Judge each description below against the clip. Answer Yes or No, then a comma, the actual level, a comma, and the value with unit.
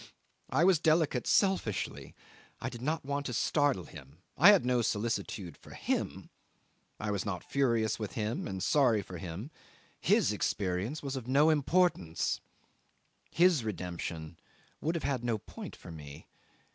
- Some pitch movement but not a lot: No, wide, 7.7 semitones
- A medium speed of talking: Yes, average, 150 wpm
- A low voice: Yes, low, 115 Hz